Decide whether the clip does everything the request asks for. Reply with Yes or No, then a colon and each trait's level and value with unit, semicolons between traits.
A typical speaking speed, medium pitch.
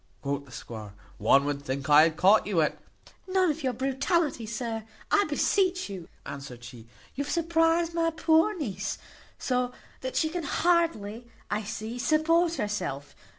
No: average, 165 wpm; high, 245 Hz